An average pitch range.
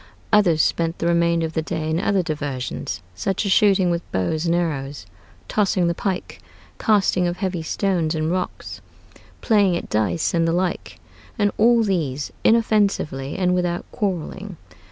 Yes: average, 3.5 semitones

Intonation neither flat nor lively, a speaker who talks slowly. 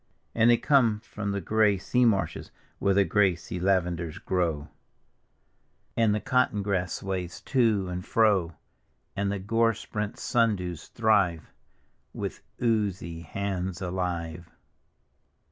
Yes: average, 3.4 semitones; slow, 125 wpm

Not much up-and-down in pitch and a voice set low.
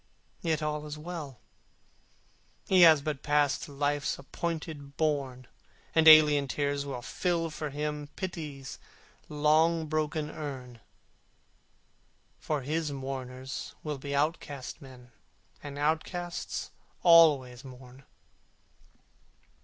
No: narrow, 2.3 semitones; medium, 150 Hz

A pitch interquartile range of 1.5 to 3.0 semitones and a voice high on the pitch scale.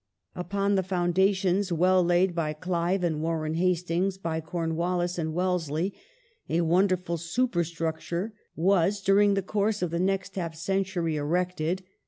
No: narrow, 2.4 semitones; medium, 180 Hz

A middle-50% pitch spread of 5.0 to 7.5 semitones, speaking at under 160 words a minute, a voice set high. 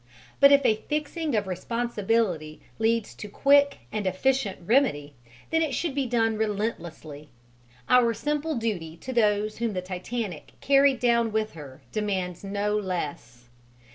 Yes: average, 5.3 semitones; average, 140 wpm; high, 220 Hz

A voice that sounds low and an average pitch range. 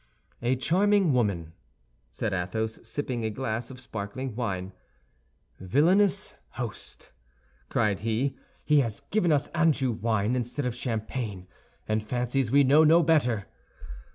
Yes: low, 120 Hz; average, 4.7 semitones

